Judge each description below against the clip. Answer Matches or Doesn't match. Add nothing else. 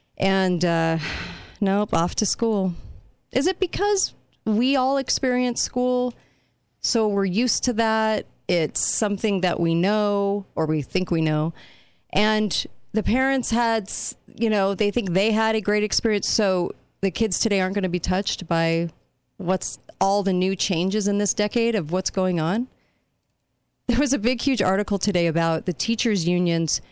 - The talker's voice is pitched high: Matches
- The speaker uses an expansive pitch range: Doesn't match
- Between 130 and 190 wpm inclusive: Matches